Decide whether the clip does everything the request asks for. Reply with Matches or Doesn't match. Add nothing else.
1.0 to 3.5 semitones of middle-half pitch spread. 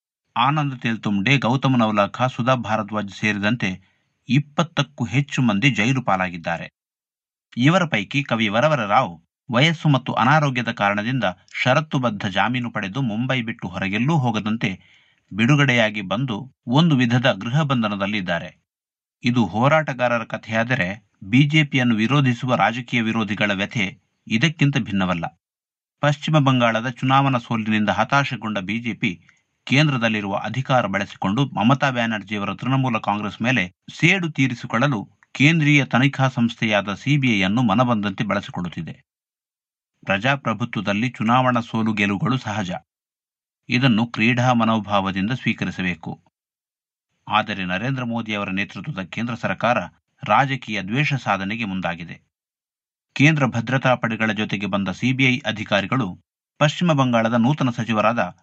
Doesn't match